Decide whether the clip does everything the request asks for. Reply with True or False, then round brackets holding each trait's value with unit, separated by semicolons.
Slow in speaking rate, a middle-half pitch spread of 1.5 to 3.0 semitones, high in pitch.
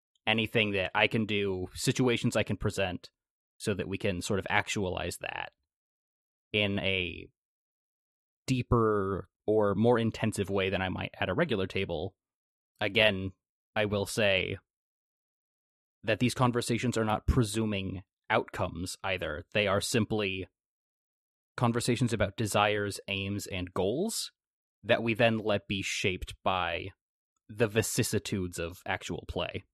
False (130 wpm; 2.7 semitones; 105 Hz)